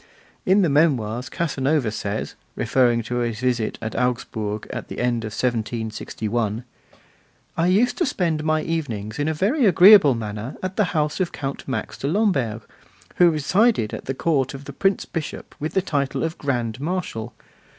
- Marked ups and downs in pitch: Yes, wide, 6.4 semitones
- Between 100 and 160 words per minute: No, average, 170 wpm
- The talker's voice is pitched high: No, low, 135 Hz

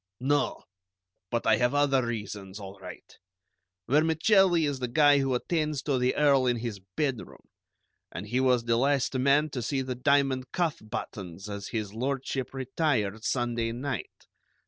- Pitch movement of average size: Yes, average, 3.9 semitones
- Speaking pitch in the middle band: No, low, 130 Hz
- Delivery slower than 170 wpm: Yes, average, 155 wpm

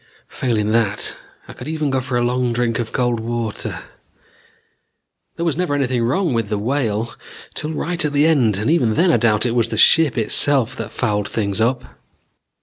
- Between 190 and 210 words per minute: Yes, average, 195 wpm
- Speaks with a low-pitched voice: Yes, low, 120 Hz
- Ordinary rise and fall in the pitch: Yes, average, 4.4 semitones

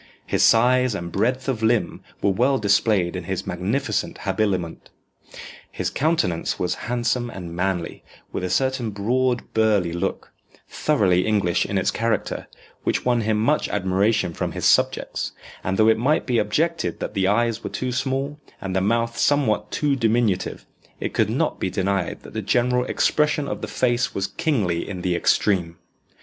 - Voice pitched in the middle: No, low, 110 Hz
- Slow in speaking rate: No, average, 165 wpm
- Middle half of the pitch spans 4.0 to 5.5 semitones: Yes, average, 4.7 semitones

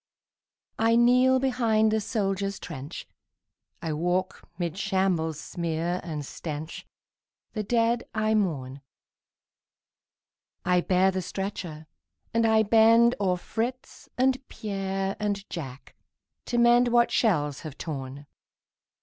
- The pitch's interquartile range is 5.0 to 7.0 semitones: Yes, wide, 5.4 semitones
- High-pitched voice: Yes, high, 195 Hz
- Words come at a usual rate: No, slow, 115 wpm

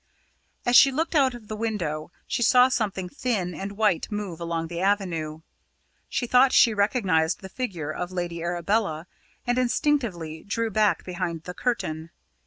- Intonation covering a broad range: Yes, wide, 5.8 semitones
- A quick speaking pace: No, average, 160 wpm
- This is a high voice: Yes, high, 195 Hz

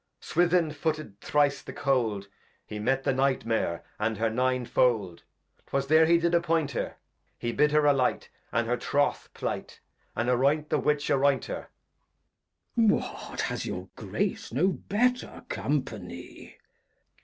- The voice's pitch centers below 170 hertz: Yes, low, 135 Hz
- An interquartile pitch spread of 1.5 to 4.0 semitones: No, average, 4.8 semitones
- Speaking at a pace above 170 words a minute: No, average, 145 wpm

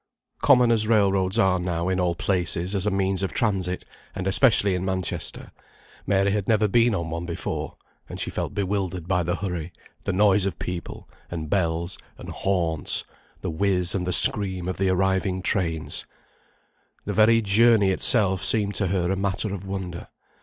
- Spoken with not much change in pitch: Yes, narrow, 2.1 semitones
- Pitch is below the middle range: Yes, very low, 95 Hz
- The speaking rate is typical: Yes, average, 175 wpm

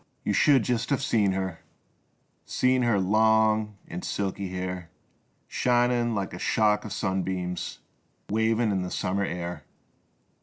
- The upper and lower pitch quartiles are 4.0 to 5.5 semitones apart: No, average, 3.4 semitones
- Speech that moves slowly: Yes, slow, 130 wpm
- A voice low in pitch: Yes, low, 105 Hz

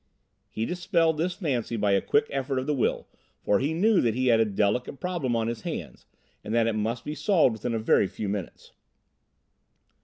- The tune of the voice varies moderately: No, wide, 6.3 semitones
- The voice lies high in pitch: No, low, 125 Hz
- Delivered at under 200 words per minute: No, fast, 205 wpm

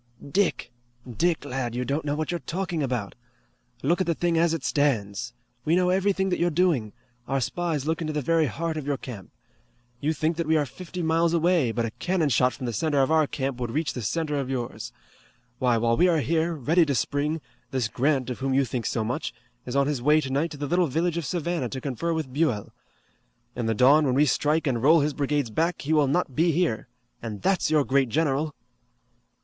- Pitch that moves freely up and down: No, average, 4.4 semitones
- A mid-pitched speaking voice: Yes, medium, 145 Hz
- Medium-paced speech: No, fast, 220 wpm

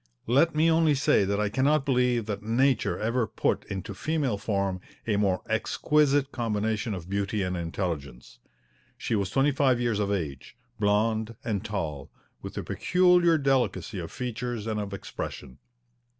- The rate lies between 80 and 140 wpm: No, average, 155 wpm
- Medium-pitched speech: No, low, 110 Hz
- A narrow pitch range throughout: No, average, 5.1 semitones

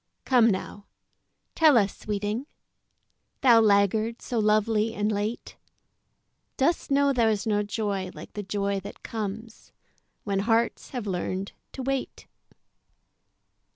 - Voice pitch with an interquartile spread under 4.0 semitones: Yes, narrow, 2.5 semitones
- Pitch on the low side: No, high, 215 Hz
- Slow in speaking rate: Yes, slow, 120 wpm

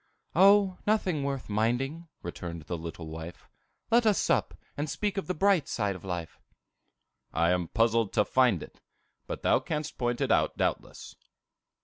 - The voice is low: Yes, low, 120 Hz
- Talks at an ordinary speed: Yes, average, 160 wpm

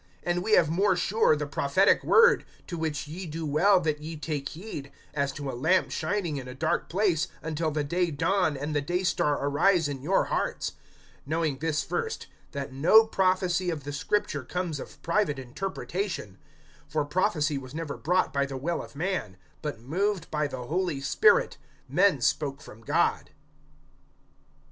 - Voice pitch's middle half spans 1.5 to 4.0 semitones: No, average, 4.4 semitones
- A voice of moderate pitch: Yes, medium, 160 Hz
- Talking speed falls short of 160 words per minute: No, average, 170 wpm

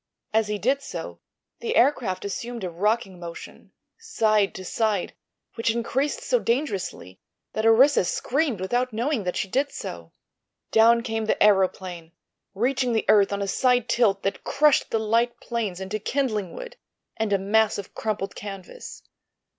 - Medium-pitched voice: No, high, 220 Hz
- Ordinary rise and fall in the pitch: Yes, average, 3.9 semitones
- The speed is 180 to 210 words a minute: No, average, 155 wpm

